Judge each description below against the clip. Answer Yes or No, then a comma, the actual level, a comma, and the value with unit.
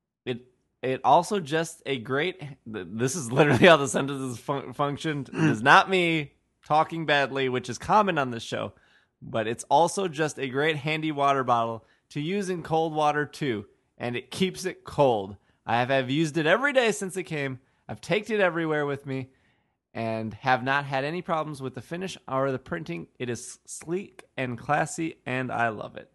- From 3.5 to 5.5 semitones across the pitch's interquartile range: Yes, average, 4.3 semitones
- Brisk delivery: No, average, 190 wpm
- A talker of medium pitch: Yes, medium, 145 Hz